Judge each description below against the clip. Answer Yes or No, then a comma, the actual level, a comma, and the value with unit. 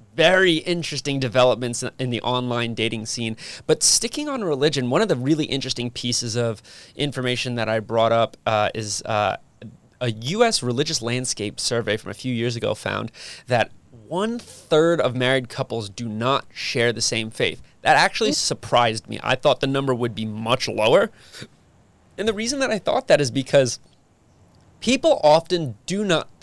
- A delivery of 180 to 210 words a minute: No, average, 170 wpm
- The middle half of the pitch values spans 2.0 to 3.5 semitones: No, average, 4.6 semitones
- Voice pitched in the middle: No, low, 125 Hz